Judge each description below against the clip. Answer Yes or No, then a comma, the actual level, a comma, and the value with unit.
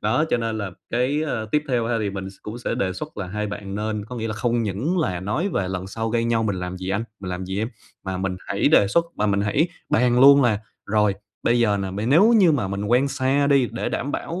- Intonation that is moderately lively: Yes, average, 4.5 semitones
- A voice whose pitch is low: Yes, low, 110 Hz